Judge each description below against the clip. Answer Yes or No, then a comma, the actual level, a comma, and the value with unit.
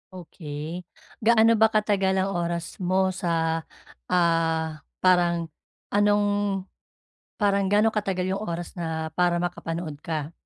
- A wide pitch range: No, average, 3.1 semitones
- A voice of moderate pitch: Yes, medium, 180 Hz